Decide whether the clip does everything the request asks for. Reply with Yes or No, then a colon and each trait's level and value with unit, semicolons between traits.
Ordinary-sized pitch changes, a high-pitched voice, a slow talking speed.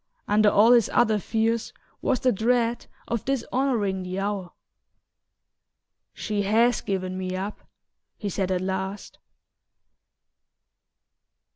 Yes: average, 3.4 semitones; high, 210 Hz; slow, 110 wpm